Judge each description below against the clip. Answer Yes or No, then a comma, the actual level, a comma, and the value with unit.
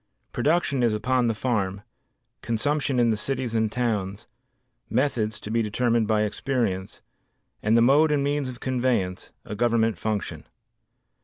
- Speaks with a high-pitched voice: No, low, 115 Hz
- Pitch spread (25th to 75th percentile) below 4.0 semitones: Yes, average, 3.3 semitones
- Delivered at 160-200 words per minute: No, average, 145 wpm